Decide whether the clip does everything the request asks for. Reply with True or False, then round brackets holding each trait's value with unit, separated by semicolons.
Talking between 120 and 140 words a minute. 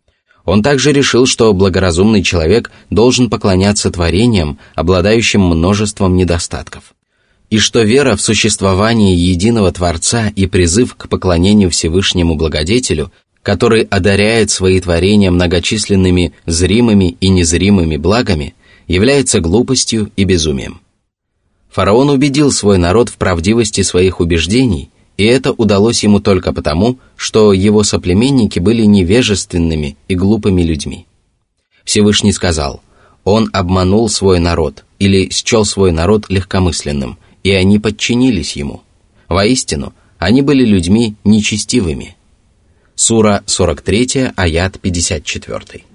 False (110 wpm)